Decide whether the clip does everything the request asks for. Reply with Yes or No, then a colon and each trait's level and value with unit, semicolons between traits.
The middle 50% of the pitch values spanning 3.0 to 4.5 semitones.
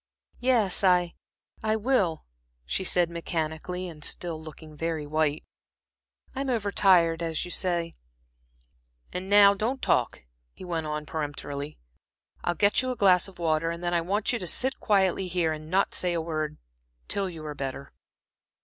Yes: average, 3.6 semitones